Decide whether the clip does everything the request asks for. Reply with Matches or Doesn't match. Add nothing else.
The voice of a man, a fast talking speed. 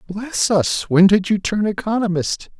Doesn't match